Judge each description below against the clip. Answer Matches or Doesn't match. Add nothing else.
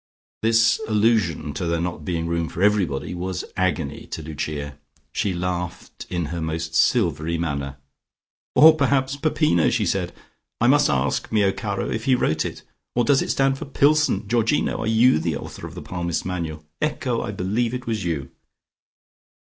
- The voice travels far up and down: Matches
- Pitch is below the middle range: Matches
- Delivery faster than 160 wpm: Matches